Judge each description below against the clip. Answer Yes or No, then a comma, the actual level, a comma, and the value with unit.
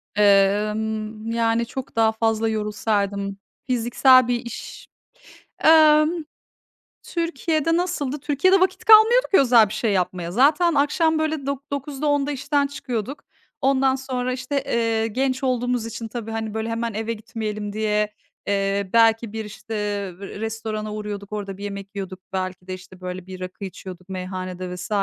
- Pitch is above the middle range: Yes, high, 225 Hz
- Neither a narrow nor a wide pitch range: Yes, average, 4.8 semitones